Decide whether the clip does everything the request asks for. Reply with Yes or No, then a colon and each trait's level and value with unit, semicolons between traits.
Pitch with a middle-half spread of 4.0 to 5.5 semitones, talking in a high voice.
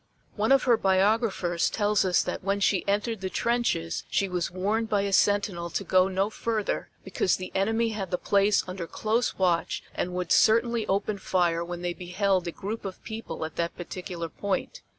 No: average, 3.1 semitones; high, 195 Hz